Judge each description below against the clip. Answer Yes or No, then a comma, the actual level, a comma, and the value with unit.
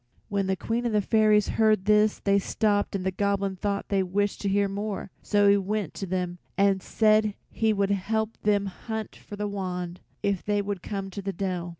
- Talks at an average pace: No, fast, 210 wpm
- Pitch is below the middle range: No, high, 200 Hz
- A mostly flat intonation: Yes, narrow, 1.5 semitones